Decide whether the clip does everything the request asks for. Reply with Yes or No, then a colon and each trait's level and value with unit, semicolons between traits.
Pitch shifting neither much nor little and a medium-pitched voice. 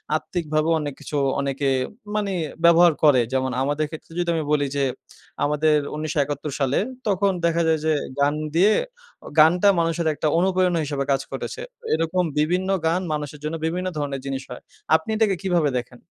Yes: average, 3.3 semitones; medium, 155 Hz